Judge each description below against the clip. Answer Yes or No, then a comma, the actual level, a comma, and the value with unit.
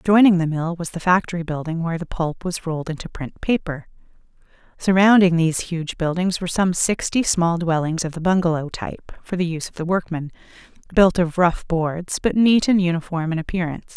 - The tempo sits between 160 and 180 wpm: No, average, 190 wpm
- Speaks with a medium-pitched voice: Yes, medium, 170 Hz